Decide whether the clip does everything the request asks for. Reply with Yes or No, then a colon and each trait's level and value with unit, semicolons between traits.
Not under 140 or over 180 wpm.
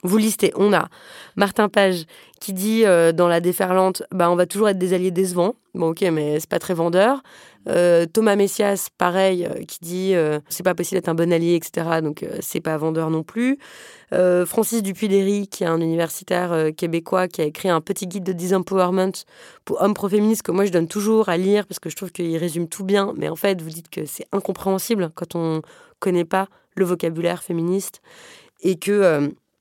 No: average, 205 wpm